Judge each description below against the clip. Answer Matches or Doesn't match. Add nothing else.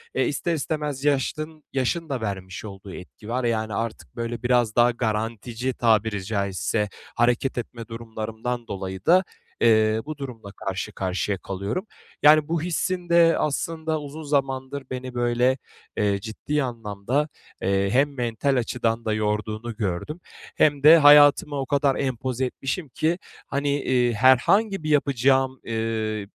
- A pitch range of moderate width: Matches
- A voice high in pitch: Doesn't match